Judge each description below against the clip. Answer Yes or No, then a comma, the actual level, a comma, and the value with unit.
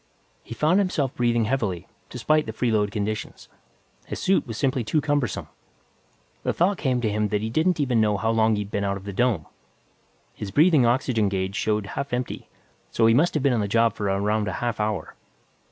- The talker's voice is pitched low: Yes, low, 115 Hz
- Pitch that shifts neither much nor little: Yes, average, 4.2 semitones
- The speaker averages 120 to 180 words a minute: No, average, 200 wpm